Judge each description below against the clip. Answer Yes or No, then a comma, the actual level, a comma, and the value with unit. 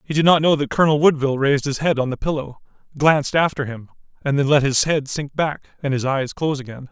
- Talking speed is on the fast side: Yes, fast, 245 wpm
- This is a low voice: No, medium, 145 Hz